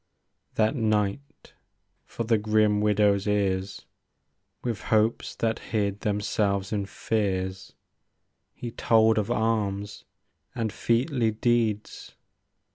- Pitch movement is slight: Yes, narrow, 1.9 semitones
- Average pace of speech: No, slow, 100 wpm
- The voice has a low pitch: Yes, low, 105 Hz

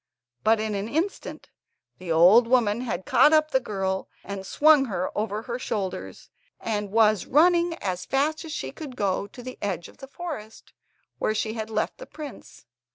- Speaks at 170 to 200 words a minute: Yes, average, 180 wpm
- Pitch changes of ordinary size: No, wide, 5.8 semitones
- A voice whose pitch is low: No, high, 220 Hz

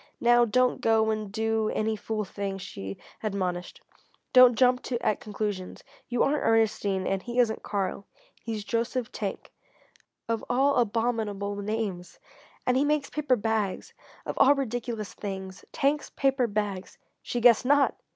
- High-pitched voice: Yes, high, 220 Hz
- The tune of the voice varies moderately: Yes, average, 3.4 semitones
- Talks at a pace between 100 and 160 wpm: Yes, average, 140 wpm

